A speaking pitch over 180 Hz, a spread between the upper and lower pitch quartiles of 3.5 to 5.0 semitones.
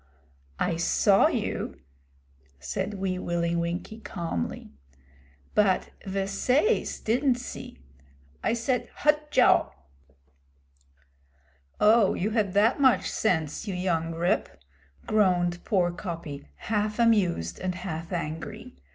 Yes: high, 190 Hz; average, 4.2 semitones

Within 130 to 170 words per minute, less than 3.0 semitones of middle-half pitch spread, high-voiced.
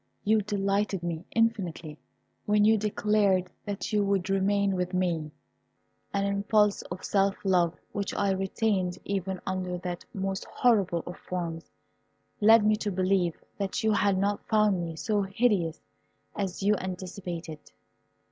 Yes: average, 140 wpm; narrow, 2.4 semitones; high, 195 Hz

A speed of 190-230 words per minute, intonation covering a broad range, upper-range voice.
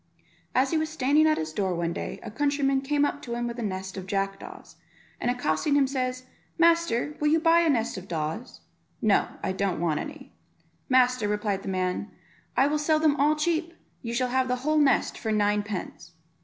Yes: fast, 205 wpm; wide, 6.7 semitones; very high, 250 Hz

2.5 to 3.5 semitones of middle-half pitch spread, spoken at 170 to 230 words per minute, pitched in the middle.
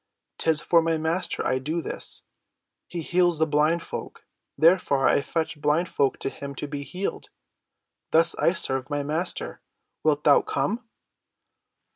No: average, 2.9 semitones; average, 145 wpm; medium, 155 Hz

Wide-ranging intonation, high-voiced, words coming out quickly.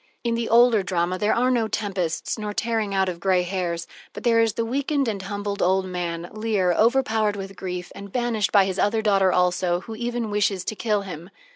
No: average, 3.5 semitones; high, 205 Hz; fast, 210 wpm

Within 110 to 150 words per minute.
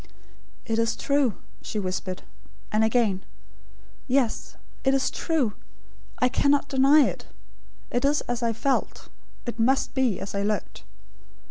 Yes: slow, 135 wpm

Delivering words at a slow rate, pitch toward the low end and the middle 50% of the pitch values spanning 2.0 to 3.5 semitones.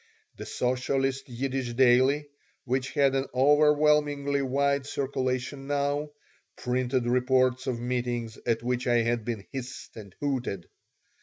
Yes: slow, 125 wpm; low, 130 Hz; narrow, 2.4 semitones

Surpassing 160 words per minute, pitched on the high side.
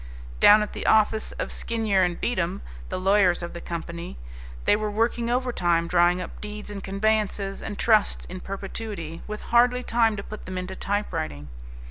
Yes: average, 170 wpm; high, 200 Hz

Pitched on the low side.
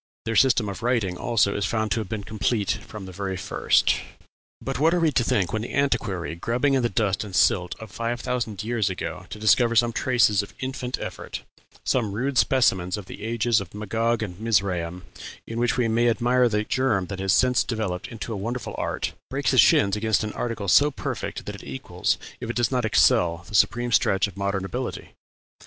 Yes: low, 110 Hz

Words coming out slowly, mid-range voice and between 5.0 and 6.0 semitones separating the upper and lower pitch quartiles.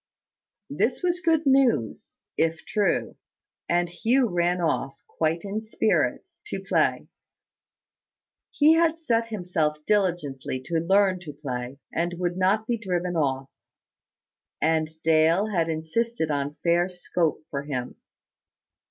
Yes: slow, 125 wpm; medium, 175 Hz; average, 5.3 semitones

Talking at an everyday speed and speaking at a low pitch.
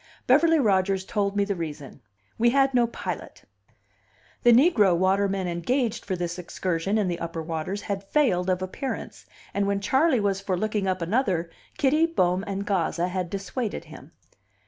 No: average, 165 wpm; high, 195 Hz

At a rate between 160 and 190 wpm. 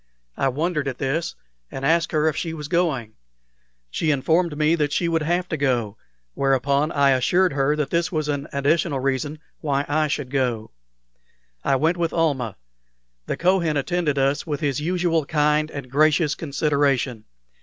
Yes: average, 165 wpm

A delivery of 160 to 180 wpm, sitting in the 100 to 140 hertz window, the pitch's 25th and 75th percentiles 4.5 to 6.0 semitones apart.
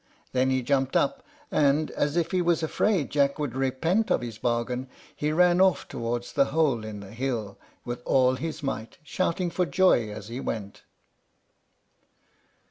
Yes: average, 165 wpm; low, 135 Hz; wide, 5.4 semitones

